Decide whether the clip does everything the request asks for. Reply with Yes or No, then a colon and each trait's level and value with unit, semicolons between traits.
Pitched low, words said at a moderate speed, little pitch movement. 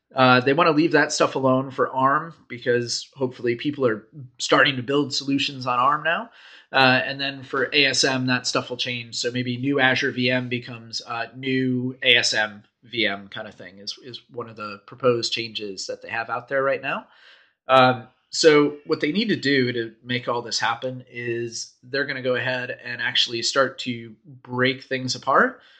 Yes: low, 125 Hz; average, 190 wpm; narrow, 2.3 semitones